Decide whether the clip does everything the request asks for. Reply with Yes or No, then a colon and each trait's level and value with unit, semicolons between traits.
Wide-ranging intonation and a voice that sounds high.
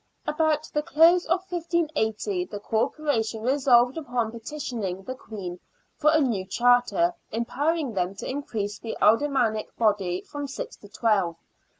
Yes: wide, 6.0 semitones; high, 245 Hz